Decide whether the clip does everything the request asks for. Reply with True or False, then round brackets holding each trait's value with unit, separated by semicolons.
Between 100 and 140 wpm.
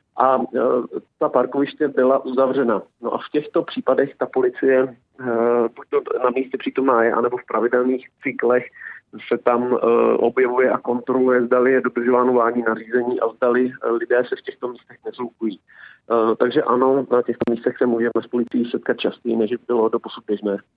False (160 wpm)